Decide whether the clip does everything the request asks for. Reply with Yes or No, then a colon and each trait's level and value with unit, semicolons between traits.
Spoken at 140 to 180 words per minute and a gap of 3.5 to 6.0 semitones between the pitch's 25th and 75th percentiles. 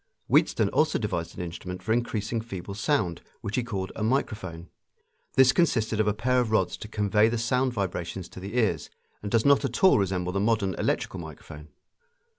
No: average, 190 wpm; average, 4.1 semitones